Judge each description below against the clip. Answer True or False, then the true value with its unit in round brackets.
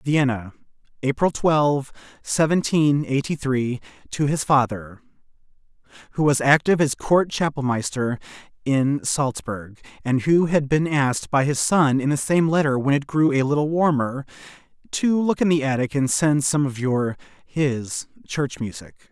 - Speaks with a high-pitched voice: False (140 Hz)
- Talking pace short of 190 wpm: True (150 wpm)